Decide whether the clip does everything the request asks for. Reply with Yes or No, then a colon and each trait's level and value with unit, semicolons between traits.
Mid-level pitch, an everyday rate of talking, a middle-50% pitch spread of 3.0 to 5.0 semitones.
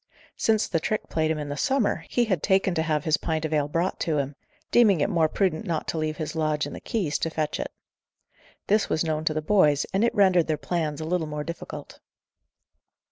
No: medium, 160 Hz; fast, 230 wpm; average, 3.8 semitones